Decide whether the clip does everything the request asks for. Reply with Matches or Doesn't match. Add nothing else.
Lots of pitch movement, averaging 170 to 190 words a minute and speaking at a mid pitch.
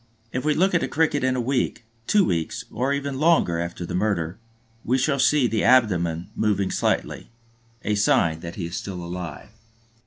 Doesn't match